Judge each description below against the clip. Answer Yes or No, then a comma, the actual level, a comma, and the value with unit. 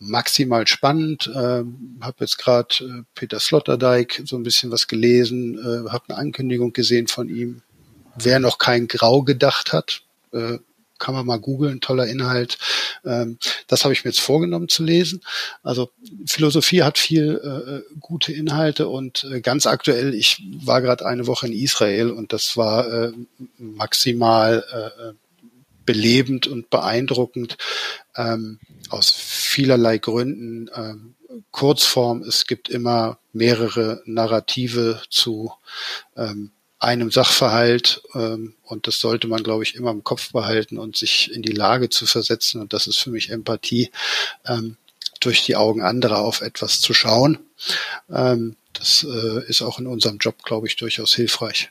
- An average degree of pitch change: No, narrow, 2.1 semitones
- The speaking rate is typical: Yes, average, 150 wpm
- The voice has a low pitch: Yes, low, 120 Hz